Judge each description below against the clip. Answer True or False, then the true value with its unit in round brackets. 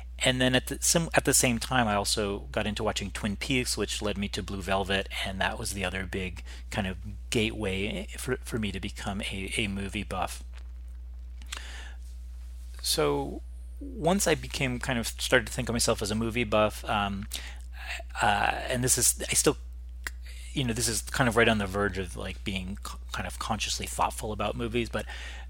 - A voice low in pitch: True (100 Hz)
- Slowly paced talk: False (195 wpm)